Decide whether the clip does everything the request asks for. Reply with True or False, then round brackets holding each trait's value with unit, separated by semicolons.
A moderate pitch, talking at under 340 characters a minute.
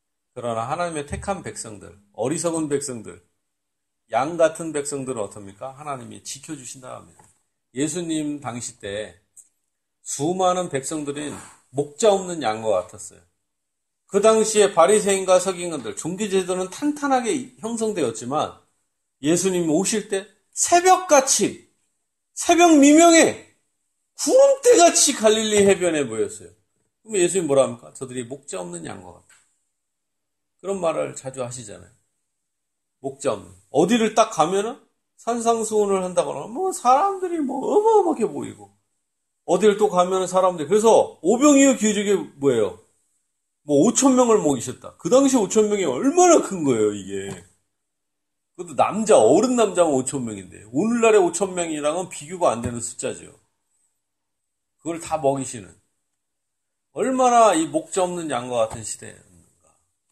True (175 Hz; 290 characters per minute)